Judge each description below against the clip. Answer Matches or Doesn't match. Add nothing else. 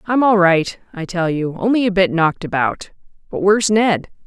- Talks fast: Doesn't match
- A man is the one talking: Doesn't match